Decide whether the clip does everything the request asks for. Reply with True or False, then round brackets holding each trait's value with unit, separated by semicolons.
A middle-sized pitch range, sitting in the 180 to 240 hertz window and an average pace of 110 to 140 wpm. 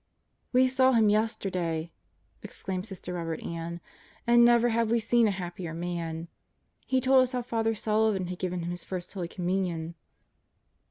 False (5.0 semitones; 190 Hz; 160 wpm)